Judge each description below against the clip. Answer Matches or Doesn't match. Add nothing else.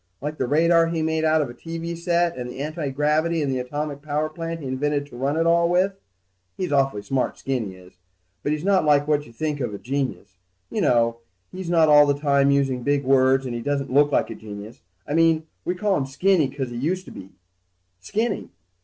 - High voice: Doesn't match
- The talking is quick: Matches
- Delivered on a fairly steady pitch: Doesn't match